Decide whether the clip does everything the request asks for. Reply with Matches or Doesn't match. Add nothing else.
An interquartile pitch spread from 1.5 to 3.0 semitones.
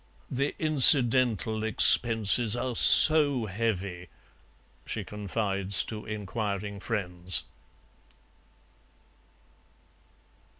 Doesn't match